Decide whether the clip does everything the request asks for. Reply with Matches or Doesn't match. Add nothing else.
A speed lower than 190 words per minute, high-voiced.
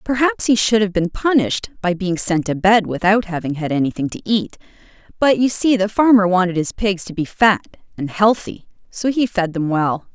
Doesn't match